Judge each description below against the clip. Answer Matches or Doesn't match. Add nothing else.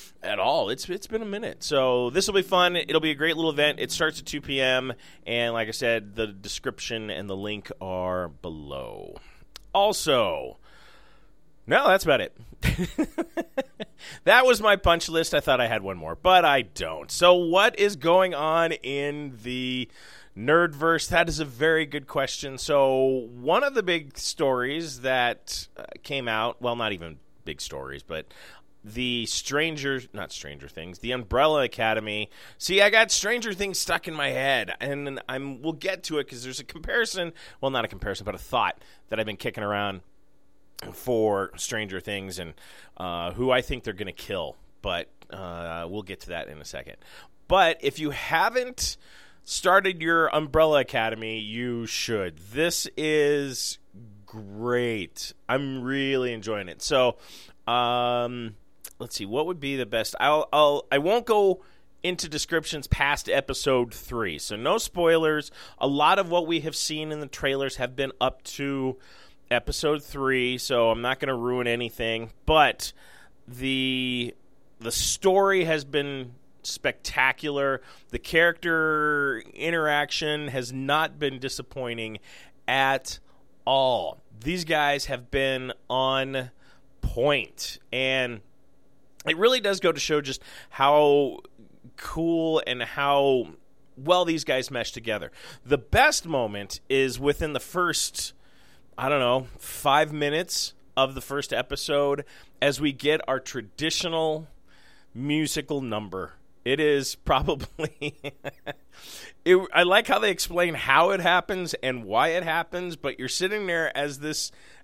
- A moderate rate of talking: Matches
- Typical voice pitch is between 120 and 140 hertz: Matches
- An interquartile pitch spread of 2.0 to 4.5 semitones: Doesn't match